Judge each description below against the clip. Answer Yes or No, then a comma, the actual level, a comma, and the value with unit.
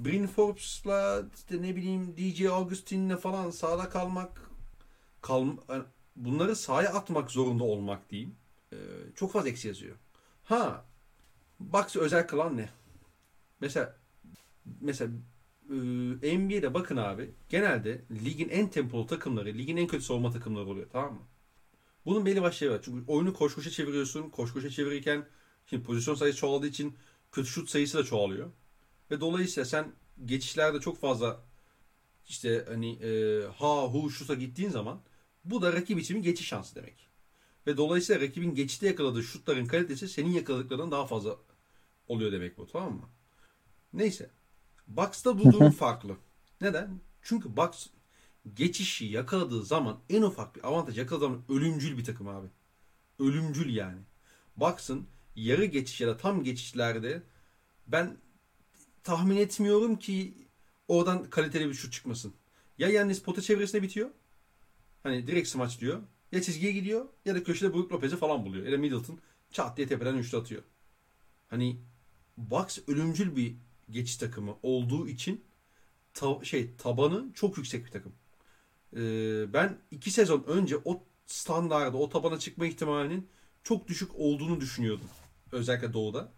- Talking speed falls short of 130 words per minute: No, fast, 140 wpm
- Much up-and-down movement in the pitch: Yes, wide, 6.7 semitones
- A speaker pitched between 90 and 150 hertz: Yes, medium, 145 Hz